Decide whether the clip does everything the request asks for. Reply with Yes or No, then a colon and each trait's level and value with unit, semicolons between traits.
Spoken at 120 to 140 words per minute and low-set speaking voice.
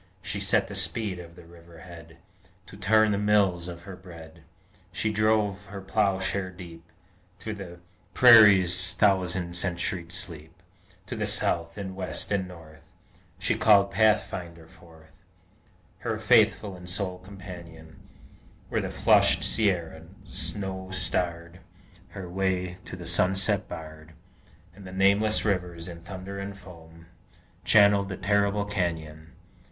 Yes: slow, 135 wpm; very low, 95 Hz